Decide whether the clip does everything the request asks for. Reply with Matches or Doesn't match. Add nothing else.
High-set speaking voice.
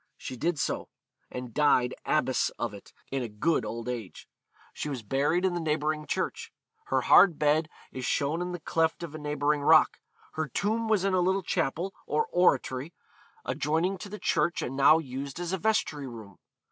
Doesn't match